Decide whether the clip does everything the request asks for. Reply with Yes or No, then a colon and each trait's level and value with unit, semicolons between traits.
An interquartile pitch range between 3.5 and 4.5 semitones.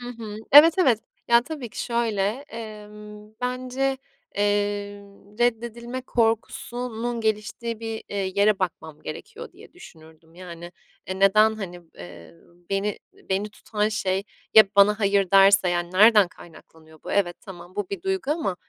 Yes: average, 3.9 semitones